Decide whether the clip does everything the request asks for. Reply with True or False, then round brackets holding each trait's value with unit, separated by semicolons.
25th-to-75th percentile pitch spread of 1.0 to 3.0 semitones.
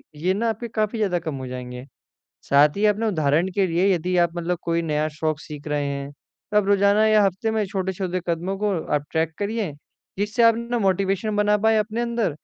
False (4.7 semitones)